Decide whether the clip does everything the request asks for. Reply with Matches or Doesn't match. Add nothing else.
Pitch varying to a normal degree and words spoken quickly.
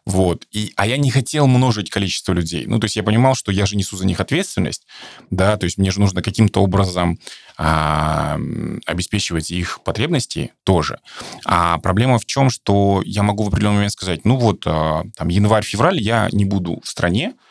Matches